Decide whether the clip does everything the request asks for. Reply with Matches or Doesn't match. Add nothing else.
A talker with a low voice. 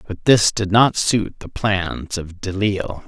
Matches